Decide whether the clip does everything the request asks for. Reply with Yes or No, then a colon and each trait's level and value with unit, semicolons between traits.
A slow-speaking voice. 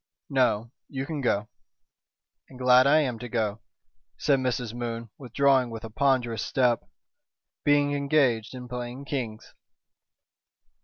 Yes: slow, 125 wpm